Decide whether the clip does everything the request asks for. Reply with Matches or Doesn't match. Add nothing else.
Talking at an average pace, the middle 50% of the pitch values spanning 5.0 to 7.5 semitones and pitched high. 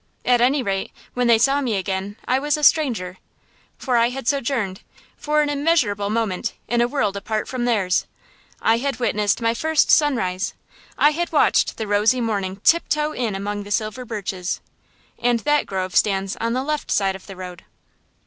Matches